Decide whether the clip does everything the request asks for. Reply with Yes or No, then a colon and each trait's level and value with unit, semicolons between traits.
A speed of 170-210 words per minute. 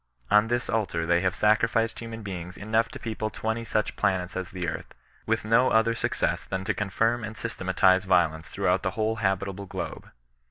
Yes: average, 190 wpm